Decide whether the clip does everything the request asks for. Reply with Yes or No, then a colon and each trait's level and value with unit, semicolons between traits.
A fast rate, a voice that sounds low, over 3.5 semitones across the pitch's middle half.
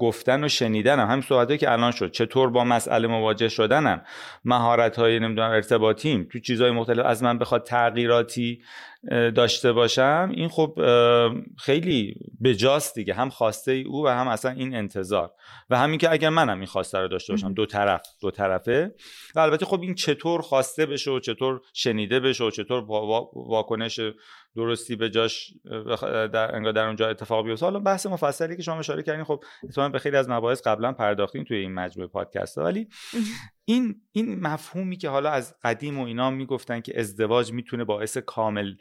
Yes: fast, 175 wpm; low, 120 Hz; average, 4.0 semitones